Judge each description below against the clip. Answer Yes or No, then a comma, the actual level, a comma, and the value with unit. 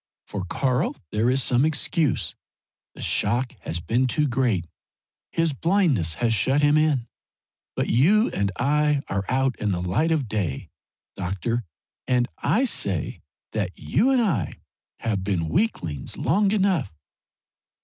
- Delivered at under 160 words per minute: Yes, average, 140 wpm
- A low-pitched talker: Yes, low, 125 Hz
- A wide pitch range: Yes, wide, 7.3 semitones